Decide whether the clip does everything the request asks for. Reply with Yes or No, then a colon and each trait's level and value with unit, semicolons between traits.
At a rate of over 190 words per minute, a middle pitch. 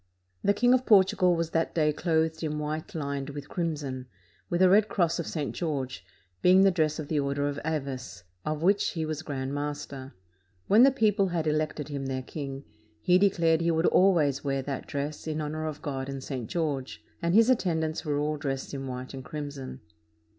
Yes: average, 200 wpm; medium, 155 Hz